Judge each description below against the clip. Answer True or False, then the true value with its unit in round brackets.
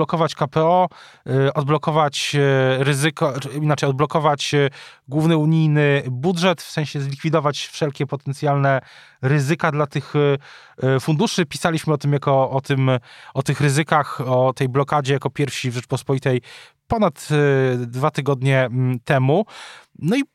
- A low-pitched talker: False (145 Hz)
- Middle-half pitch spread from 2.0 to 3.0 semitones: True (2.4 semitones)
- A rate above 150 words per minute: False (120 wpm)